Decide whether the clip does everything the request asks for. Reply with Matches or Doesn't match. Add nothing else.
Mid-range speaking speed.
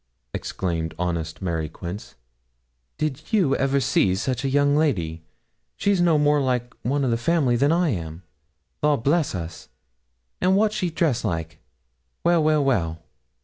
Matches